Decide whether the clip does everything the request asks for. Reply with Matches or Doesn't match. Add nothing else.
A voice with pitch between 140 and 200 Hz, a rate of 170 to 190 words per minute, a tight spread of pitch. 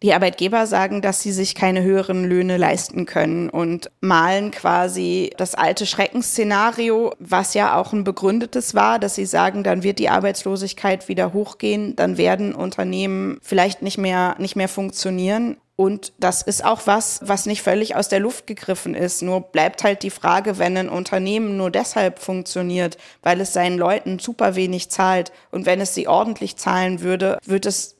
Matches